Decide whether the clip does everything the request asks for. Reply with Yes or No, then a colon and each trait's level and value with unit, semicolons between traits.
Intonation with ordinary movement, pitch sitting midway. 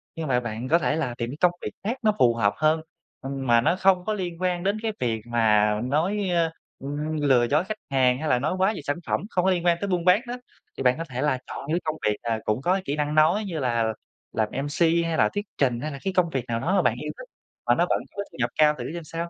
No: wide, 6.1 semitones; medium, 155 Hz